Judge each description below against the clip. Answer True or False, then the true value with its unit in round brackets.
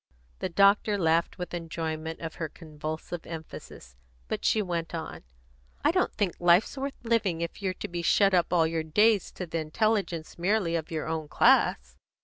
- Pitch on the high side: False (170 Hz)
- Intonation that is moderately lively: True (3.4 semitones)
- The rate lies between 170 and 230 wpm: True (175 wpm)